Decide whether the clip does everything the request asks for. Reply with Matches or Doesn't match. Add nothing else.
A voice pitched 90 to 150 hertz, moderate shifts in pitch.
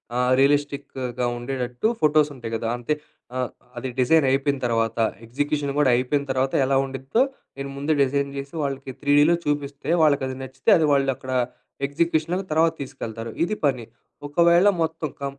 Doesn't match